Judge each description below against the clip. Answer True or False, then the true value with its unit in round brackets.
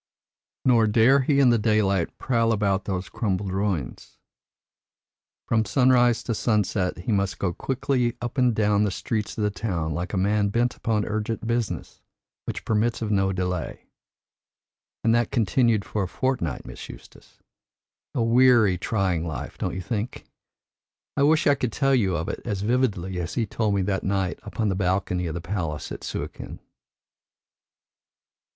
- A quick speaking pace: False (165 wpm)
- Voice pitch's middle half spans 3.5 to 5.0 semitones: True (3.8 semitones)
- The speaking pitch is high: False (105 Hz)